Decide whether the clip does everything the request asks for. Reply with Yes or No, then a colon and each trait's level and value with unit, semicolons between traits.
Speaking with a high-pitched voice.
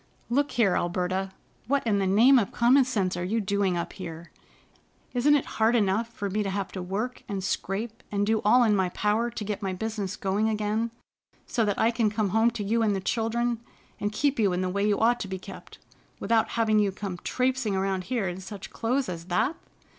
Yes: high, 210 Hz